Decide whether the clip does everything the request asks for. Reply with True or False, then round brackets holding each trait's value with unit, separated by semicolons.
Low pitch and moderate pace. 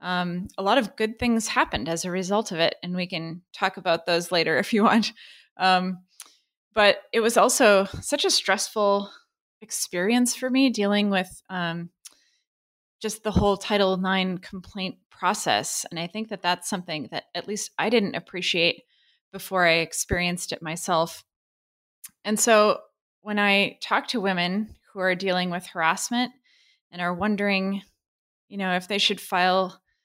False (195 Hz; 160 wpm)